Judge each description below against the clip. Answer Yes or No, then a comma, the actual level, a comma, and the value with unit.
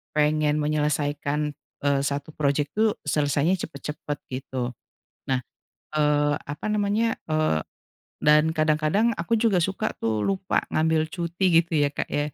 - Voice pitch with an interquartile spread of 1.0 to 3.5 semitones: Yes, average, 2.7 semitones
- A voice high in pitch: No, medium, 150 Hz